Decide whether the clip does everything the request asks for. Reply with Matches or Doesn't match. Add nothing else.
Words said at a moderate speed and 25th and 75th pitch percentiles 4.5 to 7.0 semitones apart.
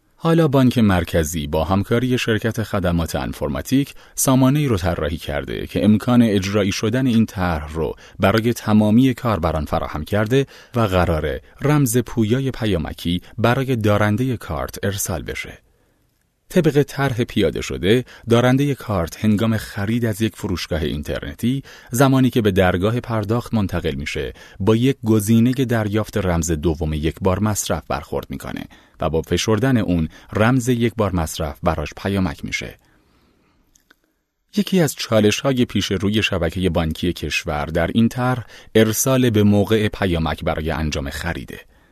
Matches